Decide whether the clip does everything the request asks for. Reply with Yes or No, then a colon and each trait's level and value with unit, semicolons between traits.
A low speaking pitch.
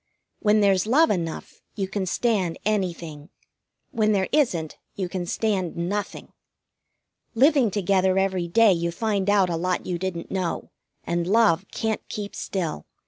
No: high, 190 Hz